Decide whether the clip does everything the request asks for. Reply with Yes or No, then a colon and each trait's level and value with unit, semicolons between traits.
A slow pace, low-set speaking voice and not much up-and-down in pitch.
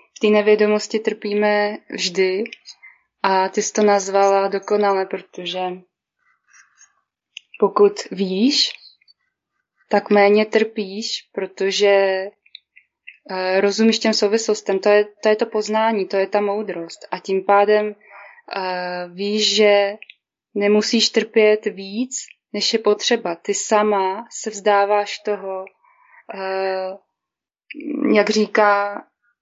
No: slow, 100 wpm; high, 205 Hz; narrow, 1.6 semitones